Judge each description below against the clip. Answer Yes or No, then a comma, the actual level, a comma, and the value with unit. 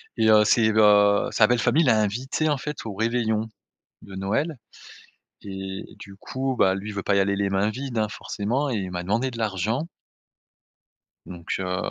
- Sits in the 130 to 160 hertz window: No, low, 105 Hz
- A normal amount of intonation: Yes, average, 3.7 semitones